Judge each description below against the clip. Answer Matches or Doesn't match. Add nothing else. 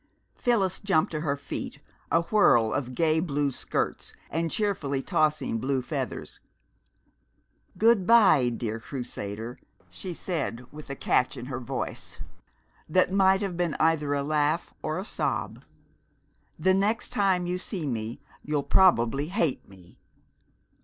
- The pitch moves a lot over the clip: Matches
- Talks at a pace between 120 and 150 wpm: Matches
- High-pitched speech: Doesn't match